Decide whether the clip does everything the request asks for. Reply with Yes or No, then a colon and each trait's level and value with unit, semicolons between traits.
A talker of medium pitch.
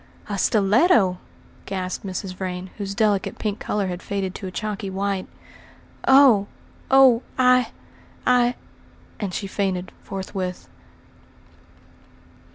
No: high, 200 Hz